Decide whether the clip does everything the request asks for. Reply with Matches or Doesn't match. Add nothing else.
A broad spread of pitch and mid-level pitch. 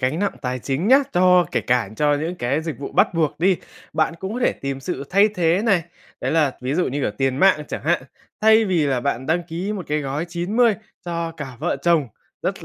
Doesn't match